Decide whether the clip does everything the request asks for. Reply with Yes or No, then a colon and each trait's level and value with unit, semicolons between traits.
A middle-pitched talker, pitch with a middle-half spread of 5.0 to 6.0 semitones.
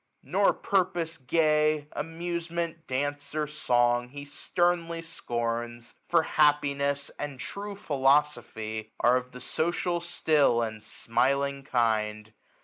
Yes: medium, 145 Hz; average, 5.3 semitones